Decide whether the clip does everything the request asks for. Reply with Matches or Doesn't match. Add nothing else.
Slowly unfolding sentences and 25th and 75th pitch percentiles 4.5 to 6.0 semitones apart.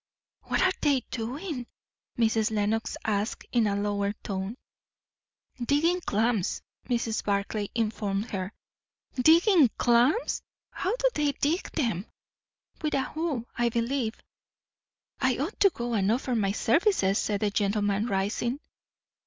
Matches